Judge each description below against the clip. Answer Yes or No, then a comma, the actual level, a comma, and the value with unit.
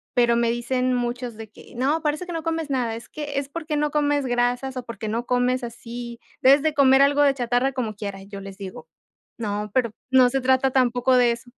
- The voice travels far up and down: No, average, 2.8 semitones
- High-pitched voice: Yes, very high, 250 Hz